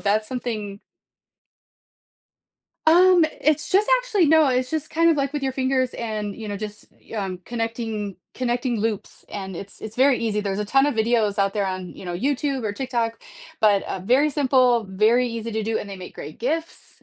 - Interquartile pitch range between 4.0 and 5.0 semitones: Yes, average, 4.5 semitones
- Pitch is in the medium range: No, high, 230 Hz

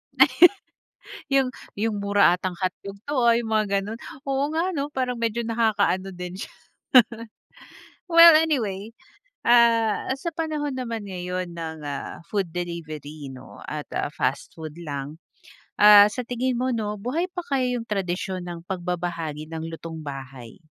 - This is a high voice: Yes, high, 195 Hz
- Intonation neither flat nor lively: No, wide, 6.1 semitones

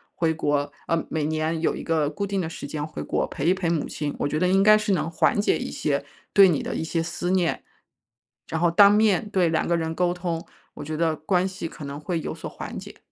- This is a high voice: No, medium, 165 Hz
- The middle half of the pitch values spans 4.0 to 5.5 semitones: No, average, 2.8 semitones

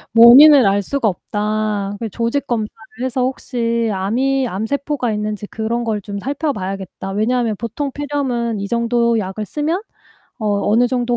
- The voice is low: No, high, 235 Hz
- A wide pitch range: No, average, 3.6 semitones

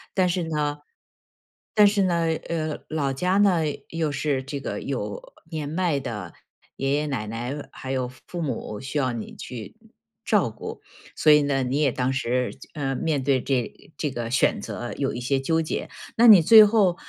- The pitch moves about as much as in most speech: Yes, average, 4.0 semitones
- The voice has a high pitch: No, medium, 145 Hz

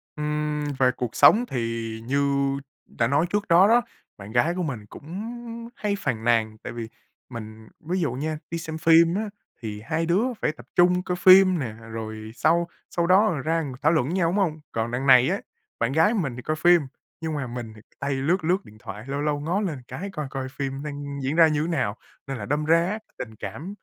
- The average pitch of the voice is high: No, medium, 150 Hz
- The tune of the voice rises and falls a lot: Yes, wide, 5.9 semitones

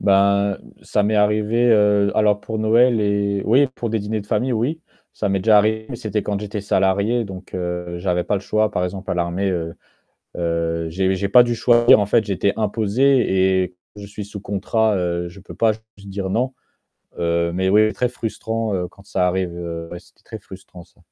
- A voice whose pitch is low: Yes, low, 100 Hz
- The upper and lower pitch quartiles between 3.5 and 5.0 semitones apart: No, average, 2.9 semitones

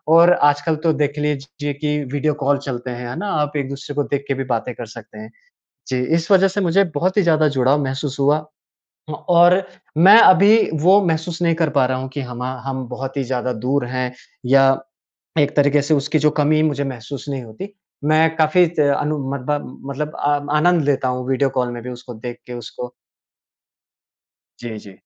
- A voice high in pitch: No, medium, 145 Hz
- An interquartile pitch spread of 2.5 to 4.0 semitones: Yes, average, 3.5 semitones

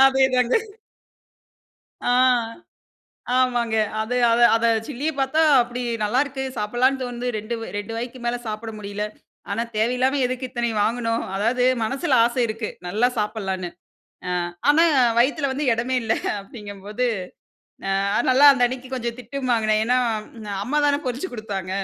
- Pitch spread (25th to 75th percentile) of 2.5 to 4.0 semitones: Yes, average, 2.9 semitones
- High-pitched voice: Yes, high, 240 Hz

